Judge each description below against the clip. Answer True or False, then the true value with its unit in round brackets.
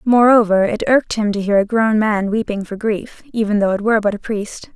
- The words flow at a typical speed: False (240 wpm)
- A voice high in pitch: True (215 Hz)